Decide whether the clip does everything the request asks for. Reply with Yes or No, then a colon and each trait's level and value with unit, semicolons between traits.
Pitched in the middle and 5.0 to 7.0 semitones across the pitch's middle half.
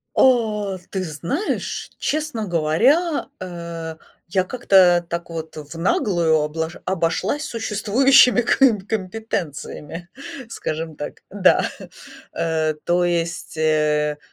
Yes: medium, 175 Hz; average, 5.3 semitones